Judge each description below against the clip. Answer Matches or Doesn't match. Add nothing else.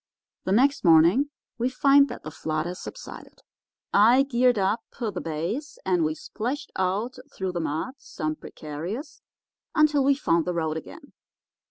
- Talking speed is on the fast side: Doesn't match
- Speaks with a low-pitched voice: Doesn't match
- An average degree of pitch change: Doesn't match